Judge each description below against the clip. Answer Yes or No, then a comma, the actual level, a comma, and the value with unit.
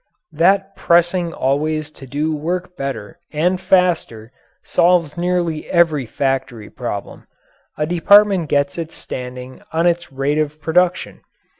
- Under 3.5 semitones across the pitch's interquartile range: No, average, 3.8 semitones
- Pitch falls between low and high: Yes, medium, 160 Hz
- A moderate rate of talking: No, slow, 125 wpm